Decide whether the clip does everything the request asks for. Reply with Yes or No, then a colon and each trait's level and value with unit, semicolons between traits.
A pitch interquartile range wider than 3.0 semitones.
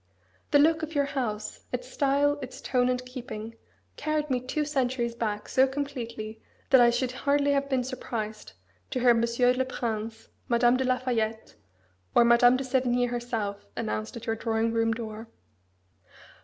No: narrow, 2.6 semitones